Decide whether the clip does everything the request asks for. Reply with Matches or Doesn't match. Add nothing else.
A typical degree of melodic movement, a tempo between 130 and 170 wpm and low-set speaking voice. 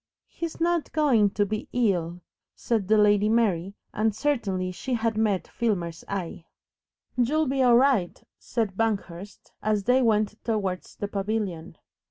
Doesn't match